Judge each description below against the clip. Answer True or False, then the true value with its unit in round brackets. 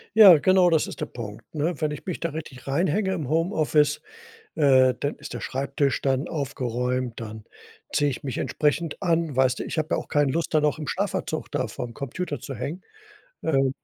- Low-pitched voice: False (145 Hz)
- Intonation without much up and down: False (3.8 semitones)